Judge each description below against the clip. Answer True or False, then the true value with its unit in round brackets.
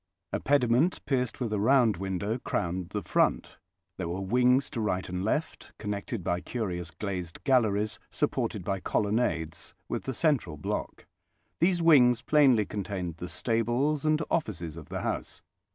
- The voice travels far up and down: True (5.7 semitones)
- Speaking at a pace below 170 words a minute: True (150 wpm)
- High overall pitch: False (105 Hz)